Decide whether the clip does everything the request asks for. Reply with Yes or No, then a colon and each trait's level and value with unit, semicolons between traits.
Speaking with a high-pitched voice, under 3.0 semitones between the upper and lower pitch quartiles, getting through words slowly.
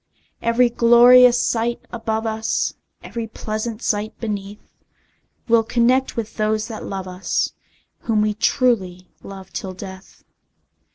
Yes: high, 220 Hz; narrow, 2.4 semitones; slow, 120 wpm